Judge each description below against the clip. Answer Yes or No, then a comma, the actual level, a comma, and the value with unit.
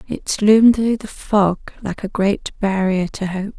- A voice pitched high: Yes, high, 200 Hz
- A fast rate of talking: No, average, 185 wpm